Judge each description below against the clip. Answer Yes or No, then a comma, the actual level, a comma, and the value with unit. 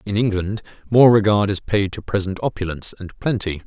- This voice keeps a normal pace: Yes, average, 180 wpm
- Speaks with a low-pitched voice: Yes, low, 100 Hz